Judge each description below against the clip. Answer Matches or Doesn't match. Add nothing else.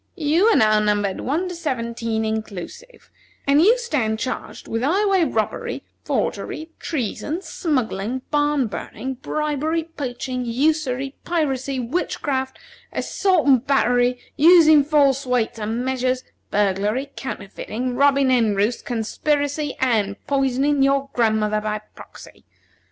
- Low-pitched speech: Doesn't match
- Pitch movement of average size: Matches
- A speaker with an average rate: Doesn't match